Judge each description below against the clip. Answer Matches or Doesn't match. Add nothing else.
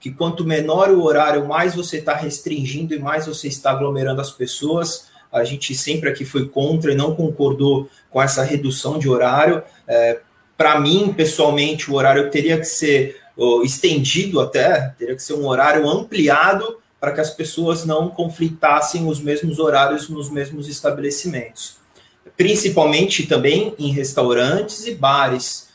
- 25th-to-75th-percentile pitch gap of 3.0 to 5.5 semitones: Doesn't match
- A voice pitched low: Doesn't match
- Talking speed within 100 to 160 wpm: Matches